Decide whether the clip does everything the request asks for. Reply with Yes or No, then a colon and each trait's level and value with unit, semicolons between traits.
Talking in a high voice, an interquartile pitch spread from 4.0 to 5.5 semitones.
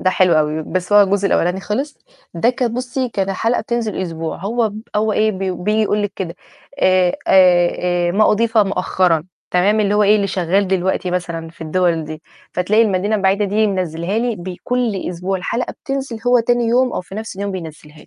No: high, 195 Hz; average, 3.4 semitones